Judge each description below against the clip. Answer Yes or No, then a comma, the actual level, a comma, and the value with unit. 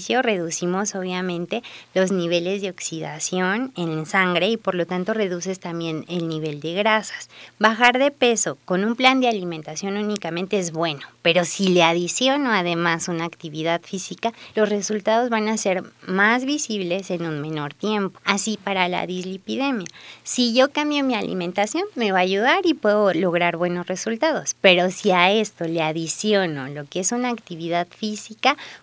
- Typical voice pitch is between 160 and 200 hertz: Yes, high, 190 Hz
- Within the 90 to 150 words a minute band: No, average, 160 wpm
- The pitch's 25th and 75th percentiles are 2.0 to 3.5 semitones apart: No, average, 3.9 semitones